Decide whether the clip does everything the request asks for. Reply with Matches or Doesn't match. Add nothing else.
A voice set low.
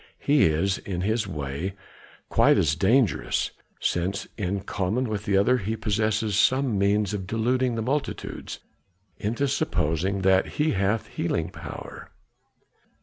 Matches